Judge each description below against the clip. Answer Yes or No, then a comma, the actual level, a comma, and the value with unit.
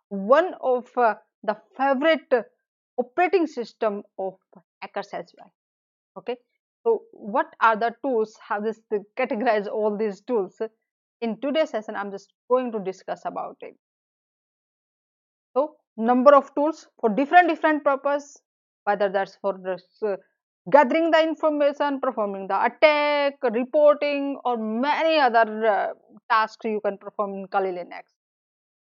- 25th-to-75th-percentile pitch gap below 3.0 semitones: No, wide, 5.5 semitones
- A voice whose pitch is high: Yes, high, 235 Hz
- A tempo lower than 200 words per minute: Yes, slow, 135 wpm